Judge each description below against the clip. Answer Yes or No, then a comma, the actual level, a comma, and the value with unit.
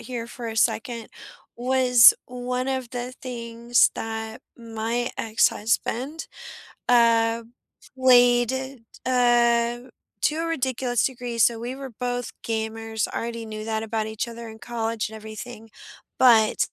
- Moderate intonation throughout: No, narrow, 1.7 semitones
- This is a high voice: Yes, high, 235 Hz